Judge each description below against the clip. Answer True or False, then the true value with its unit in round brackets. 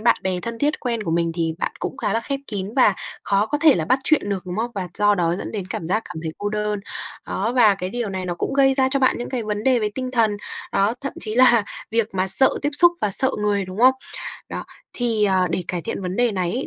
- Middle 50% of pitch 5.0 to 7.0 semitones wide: False (4.5 semitones)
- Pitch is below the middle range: False (210 Hz)